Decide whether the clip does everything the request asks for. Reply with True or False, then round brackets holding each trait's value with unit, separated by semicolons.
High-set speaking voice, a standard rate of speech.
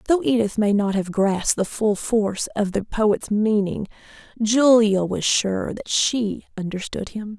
True (210 Hz; 165 wpm)